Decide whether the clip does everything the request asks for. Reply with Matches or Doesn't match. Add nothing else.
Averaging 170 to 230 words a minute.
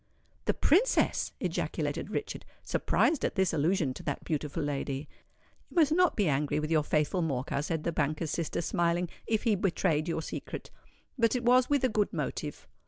Matches